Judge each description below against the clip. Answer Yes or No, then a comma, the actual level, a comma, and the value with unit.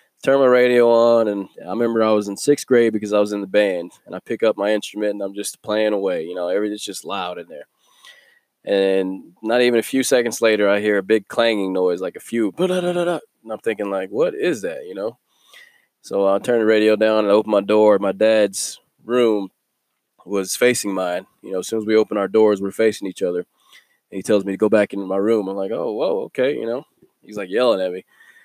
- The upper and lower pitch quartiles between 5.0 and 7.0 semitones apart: No, average, 2.7 semitones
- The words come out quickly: Yes, fast, 240 wpm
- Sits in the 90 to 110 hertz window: Yes, low, 105 Hz